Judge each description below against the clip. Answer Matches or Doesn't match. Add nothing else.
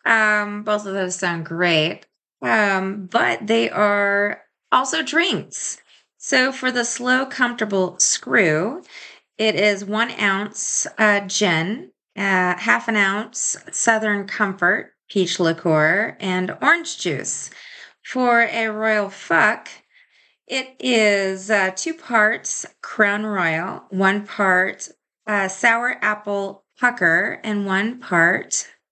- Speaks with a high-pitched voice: Matches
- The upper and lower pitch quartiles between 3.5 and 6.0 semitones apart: Doesn't match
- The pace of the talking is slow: Matches